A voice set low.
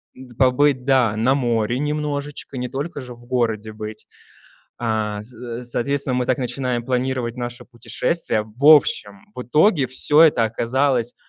Yes: low, 125 Hz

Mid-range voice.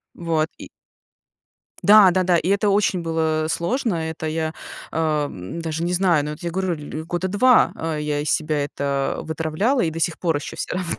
Yes: medium, 165 Hz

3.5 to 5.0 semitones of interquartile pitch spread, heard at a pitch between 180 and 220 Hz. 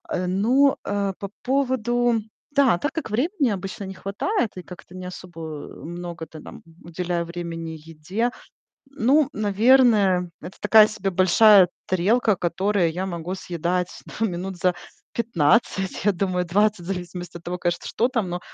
Yes: average, 4.1 semitones; high, 190 Hz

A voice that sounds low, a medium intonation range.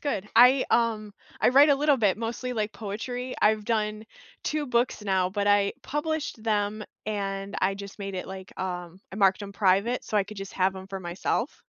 No: high, 210 Hz; average, 3.2 semitones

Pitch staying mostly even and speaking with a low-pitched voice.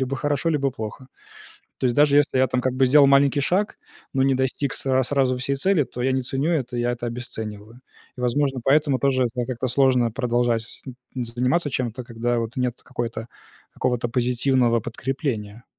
Yes: narrow, 2.3 semitones; low, 130 Hz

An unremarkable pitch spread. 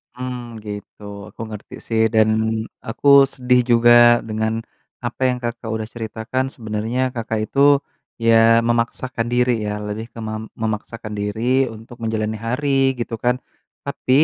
No: narrow, 2.0 semitones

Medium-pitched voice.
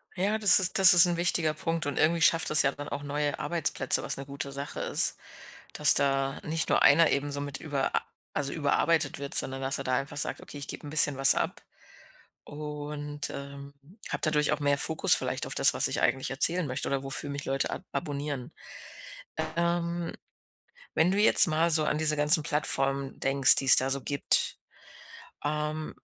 Yes: medium, 145 Hz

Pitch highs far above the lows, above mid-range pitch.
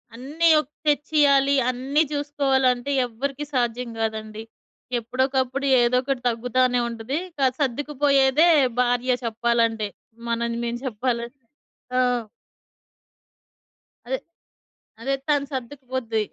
No: average, 2.9 semitones; very high, 255 Hz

